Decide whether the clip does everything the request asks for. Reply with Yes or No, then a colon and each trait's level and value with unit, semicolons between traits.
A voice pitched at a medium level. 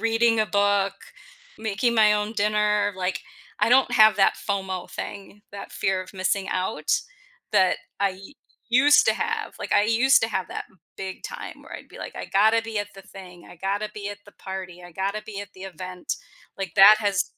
No: high, 200 Hz